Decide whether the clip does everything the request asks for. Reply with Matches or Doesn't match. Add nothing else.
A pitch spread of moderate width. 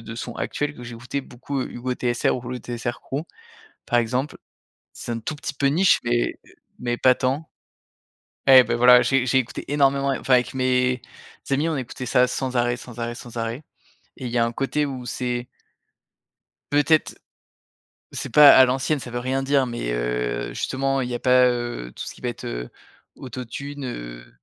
Doesn't match